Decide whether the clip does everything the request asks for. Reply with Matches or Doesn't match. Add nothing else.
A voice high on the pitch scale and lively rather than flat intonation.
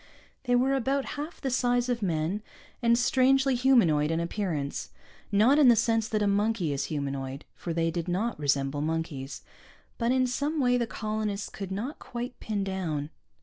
Matches